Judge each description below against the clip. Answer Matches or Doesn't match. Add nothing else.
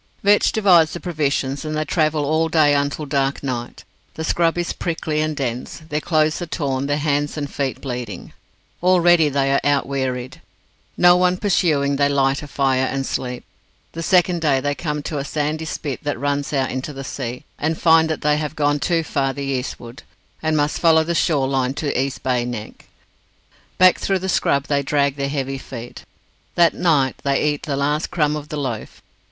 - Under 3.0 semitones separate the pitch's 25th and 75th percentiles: Matches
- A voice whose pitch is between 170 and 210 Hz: Doesn't match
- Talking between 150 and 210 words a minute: Matches